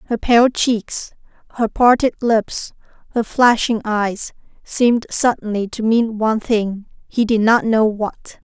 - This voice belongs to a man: No, female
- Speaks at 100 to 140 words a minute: Yes, slow, 135 wpm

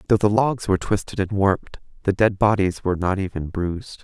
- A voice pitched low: Yes, low, 100 Hz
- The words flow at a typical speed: No, fast, 210 wpm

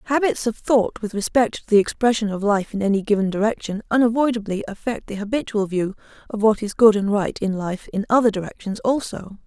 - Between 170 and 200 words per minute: Yes, average, 195 wpm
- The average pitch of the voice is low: No, high, 215 Hz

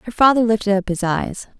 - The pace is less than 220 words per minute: No, fast, 225 wpm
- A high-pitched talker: Yes, high, 215 Hz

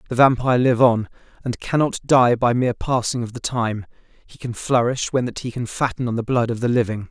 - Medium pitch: No, low, 120 Hz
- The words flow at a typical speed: No, fast, 230 wpm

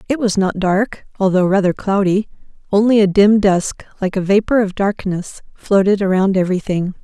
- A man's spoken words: No, female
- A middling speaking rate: Yes, average, 160 wpm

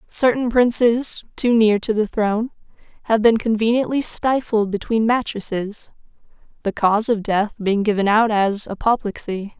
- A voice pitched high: Yes, high, 220 Hz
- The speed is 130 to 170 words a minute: Yes, average, 140 wpm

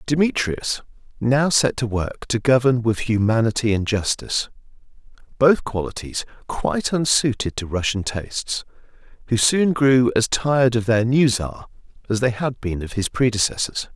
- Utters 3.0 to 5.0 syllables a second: Yes, 4.7 syllables/s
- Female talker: No, male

